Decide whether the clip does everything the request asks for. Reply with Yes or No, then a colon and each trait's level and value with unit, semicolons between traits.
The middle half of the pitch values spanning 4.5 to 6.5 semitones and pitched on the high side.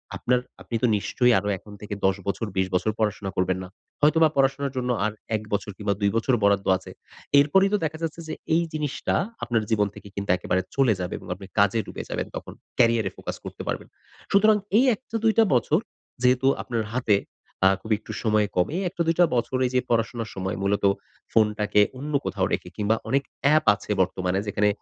No: average, 5.2 semitones; low, 115 Hz